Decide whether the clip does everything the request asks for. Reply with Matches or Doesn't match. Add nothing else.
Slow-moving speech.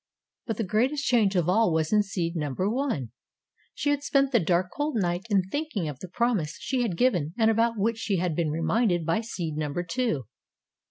Doesn't match